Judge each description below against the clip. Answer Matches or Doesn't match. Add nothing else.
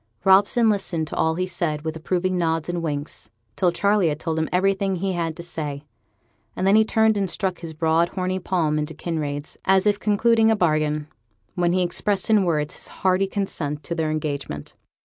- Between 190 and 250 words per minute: Matches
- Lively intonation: Doesn't match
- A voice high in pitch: Doesn't match